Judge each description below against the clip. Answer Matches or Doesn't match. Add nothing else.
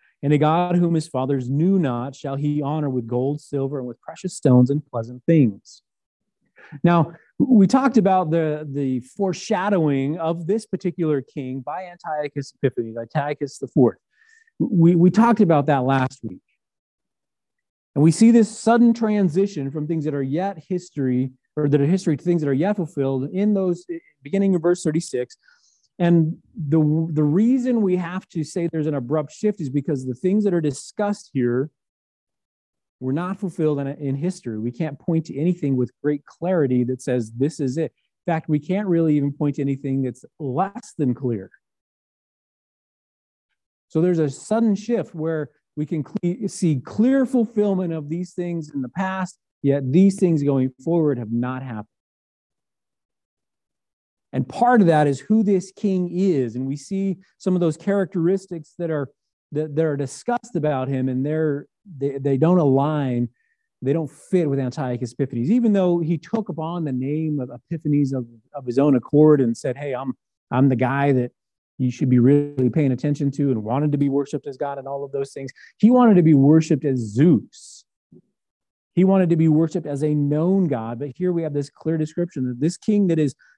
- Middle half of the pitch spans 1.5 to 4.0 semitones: Doesn't match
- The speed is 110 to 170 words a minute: Doesn't match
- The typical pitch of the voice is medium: Matches